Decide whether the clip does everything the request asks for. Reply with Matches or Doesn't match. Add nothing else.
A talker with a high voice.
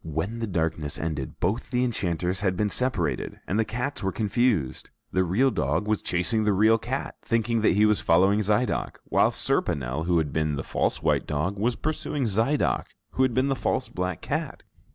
Doesn't match